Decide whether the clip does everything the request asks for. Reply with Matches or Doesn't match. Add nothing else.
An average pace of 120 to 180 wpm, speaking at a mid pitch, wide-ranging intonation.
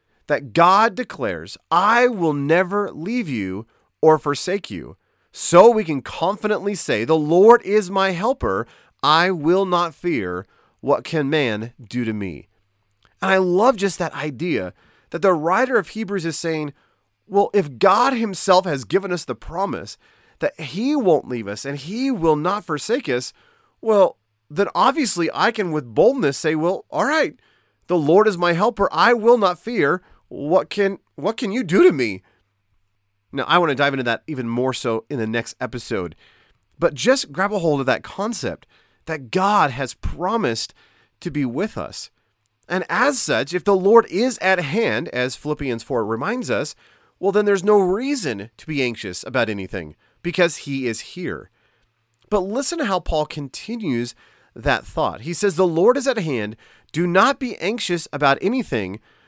Matches